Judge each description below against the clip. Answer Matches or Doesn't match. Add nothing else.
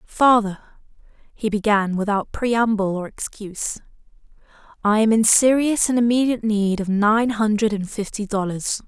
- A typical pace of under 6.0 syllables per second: Matches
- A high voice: Matches